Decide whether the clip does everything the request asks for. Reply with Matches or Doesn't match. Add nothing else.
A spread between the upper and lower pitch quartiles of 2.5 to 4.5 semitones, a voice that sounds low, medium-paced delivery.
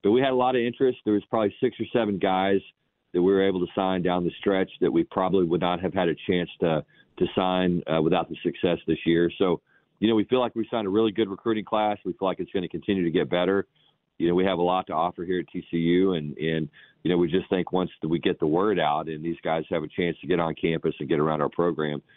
Doesn't match